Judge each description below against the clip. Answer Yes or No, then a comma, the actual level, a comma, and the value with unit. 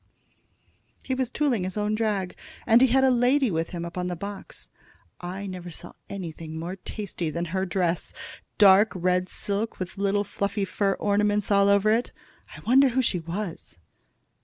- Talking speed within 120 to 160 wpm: No, average, 170 wpm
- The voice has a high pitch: Yes, high, 200 Hz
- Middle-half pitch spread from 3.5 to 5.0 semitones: No, average, 3.0 semitones